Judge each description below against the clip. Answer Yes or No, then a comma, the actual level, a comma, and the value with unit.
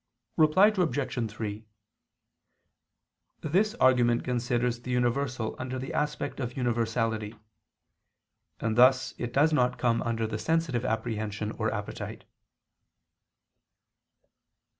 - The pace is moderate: No, slow, 100 wpm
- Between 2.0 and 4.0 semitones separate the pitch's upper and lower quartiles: Yes, average, 3.3 semitones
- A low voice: Yes, low, 120 Hz